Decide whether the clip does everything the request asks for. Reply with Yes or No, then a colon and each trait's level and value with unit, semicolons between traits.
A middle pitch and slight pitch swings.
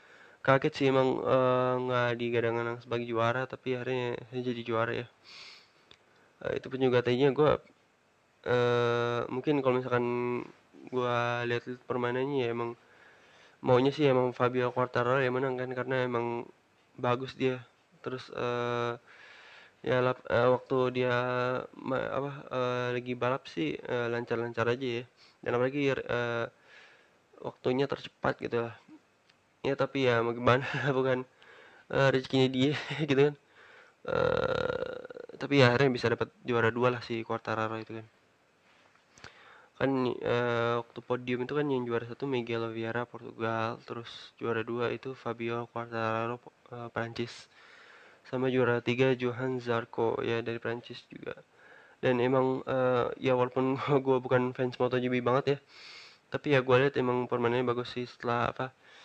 No: low, 125 Hz; narrow, 1.6 semitones